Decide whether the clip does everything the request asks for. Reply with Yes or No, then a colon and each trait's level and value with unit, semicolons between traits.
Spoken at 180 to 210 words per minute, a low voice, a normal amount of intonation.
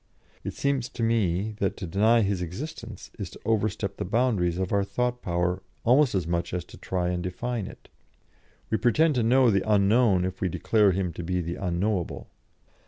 Yes: average, 190 wpm; low, 100 Hz; average, 4.5 semitones